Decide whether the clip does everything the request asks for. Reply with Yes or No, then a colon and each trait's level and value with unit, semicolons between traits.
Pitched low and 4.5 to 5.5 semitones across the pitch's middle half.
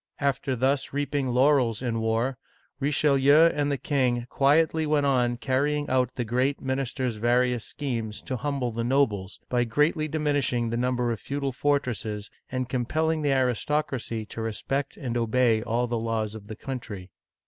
No: low, 130 Hz; average, 3.3 semitones